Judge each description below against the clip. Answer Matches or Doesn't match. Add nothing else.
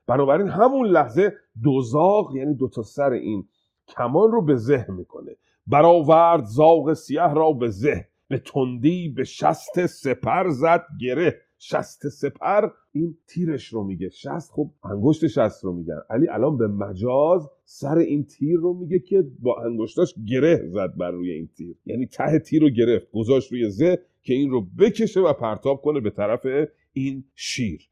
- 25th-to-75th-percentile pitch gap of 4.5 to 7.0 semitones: Matches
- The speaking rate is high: Matches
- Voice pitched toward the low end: Doesn't match